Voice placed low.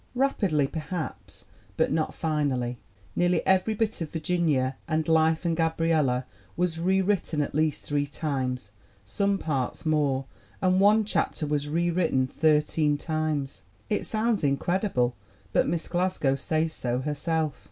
No: medium, 155 Hz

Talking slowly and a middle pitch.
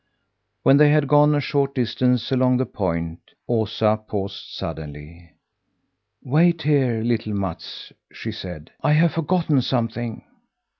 No: slow, 130 wpm; low, 120 Hz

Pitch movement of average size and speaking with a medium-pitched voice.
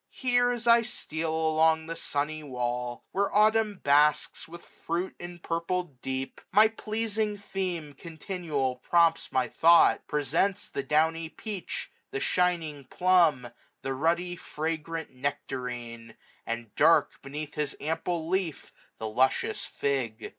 Yes: average, 4.6 semitones; medium, 160 Hz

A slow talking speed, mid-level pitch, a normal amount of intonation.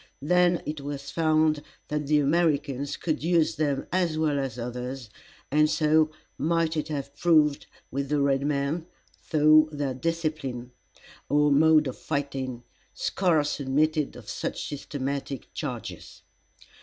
No: slow, 130 wpm; medium, 150 Hz; narrow, 2.2 semitones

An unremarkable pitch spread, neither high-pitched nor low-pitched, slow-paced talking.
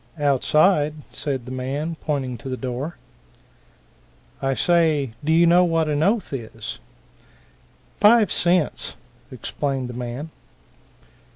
Yes: average, 4.1 semitones; medium, 145 Hz; slow, 115 wpm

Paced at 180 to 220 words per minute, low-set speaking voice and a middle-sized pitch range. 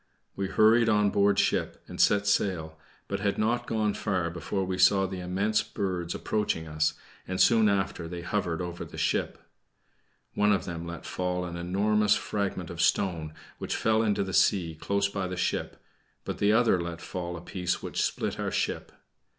Yes: average, 185 wpm; very low, 95 Hz; average, 3.0 semitones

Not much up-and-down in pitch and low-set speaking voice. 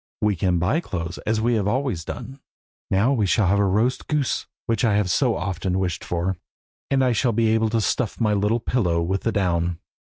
No: average, 4.1 semitones; low, 105 Hz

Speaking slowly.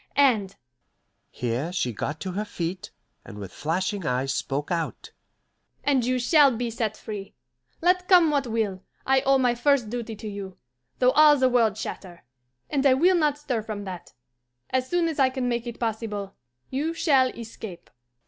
No: average, 175 wpm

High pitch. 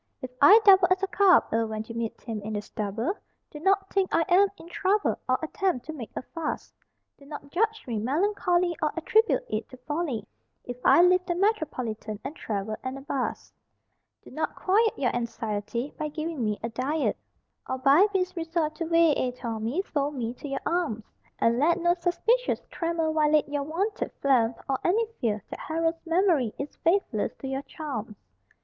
Yes: very high, 300 Hz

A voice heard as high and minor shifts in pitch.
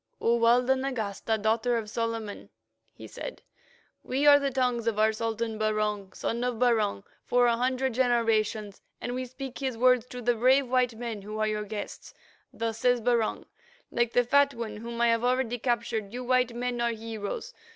Yes: high, 235 Hz; narrow, 2.2 semitones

